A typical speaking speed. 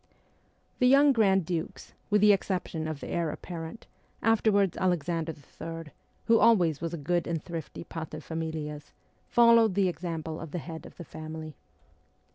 Yes: average, 150 wpm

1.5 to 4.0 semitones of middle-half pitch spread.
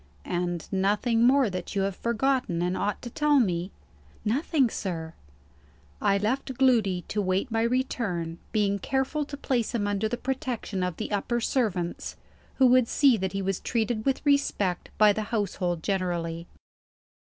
No: average, 5.3 semitones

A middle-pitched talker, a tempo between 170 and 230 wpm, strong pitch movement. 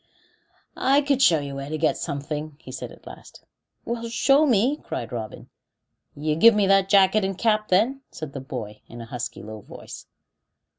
Yes: medium, 175 Hz; average, 185 wpm; wide, 8.7 semitones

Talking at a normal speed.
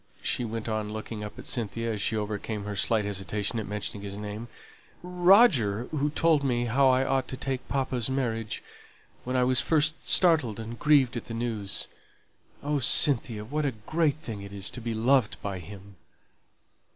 Yes: average, 180 wpm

